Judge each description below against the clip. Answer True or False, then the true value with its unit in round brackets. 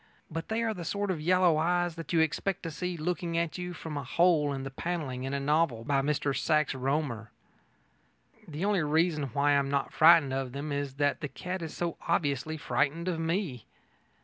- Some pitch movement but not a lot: True (3.6 semitones)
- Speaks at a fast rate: True (210 wpm)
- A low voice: False (155 Hz)